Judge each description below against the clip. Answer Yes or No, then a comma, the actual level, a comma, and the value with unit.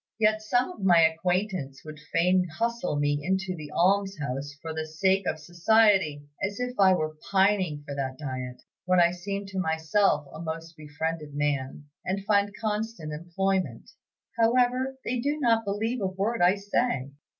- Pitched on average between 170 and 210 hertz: Yes, medium, 185 Hz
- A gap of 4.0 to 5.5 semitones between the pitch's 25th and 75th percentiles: Yes, average, 5.0 semitones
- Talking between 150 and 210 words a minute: Yes, average, 160 wpm